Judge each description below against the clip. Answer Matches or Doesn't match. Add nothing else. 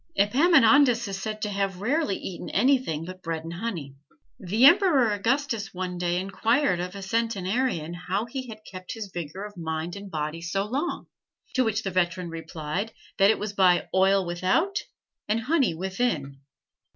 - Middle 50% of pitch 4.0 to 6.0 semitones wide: Matches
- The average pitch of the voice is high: Matches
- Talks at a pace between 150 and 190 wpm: Matches